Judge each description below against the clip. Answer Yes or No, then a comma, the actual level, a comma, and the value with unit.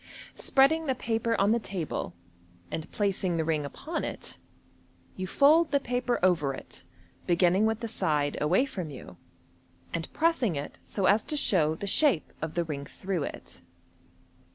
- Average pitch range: No, wide, 7.4 semitones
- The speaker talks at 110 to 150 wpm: No, average, 160 wpm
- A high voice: Yes, high, 195 Hz